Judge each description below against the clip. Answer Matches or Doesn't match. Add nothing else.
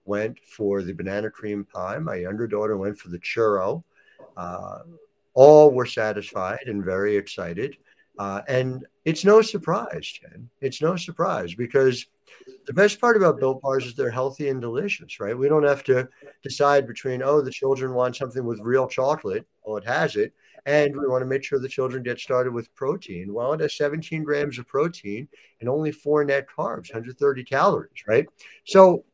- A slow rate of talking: Doesn't match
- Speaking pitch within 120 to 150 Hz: Matches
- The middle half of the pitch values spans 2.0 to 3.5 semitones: Doesn't match